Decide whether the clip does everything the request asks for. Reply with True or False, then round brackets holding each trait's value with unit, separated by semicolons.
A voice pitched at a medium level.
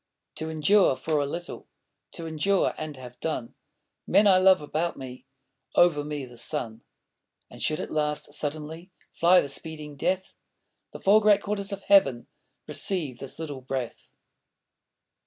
True (155 Hz)